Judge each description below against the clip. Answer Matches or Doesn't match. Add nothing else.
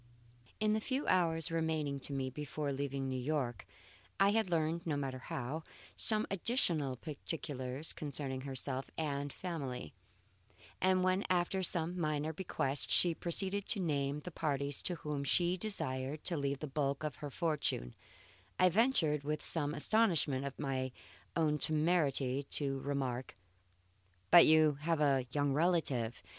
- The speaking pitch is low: Doesn't match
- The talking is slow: Doesn't match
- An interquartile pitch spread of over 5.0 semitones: Doesn't match